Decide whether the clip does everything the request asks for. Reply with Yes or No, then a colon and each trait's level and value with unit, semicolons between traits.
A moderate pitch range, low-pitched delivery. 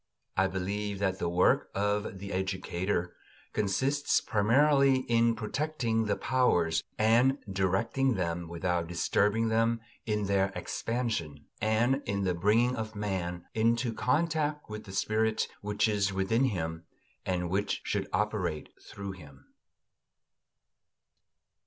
Yes: average, 3.7 semitones; low, 105 Hz